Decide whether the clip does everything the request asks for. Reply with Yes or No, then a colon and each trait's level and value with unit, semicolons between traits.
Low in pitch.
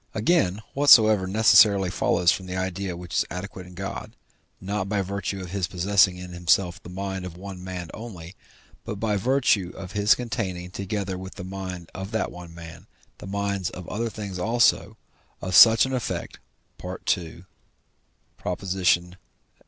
Yes: very low, 95 Hz